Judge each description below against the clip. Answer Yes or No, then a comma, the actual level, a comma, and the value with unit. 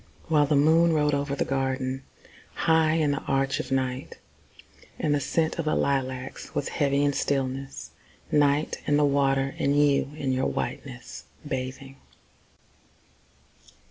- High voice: No, medium, 140 Hz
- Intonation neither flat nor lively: No, narrow, 1.6 semitones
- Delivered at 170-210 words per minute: No, average, 140 wpm